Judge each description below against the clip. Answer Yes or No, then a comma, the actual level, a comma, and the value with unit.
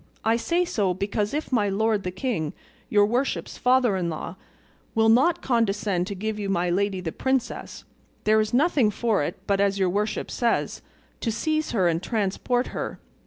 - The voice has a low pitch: No, high, 210 Hz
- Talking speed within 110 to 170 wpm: No, average, 180 wpm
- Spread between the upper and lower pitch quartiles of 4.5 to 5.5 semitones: No, average, 3.7 semitones